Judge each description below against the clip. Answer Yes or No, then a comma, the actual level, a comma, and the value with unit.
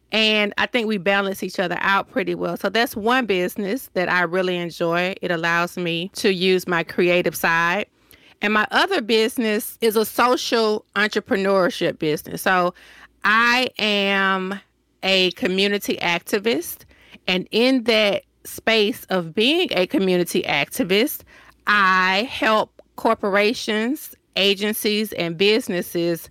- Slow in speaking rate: Yes, slow, 130 wpm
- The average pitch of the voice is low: No, high, 200 Hz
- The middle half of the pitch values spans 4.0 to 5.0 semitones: No, average, 3.6 semitones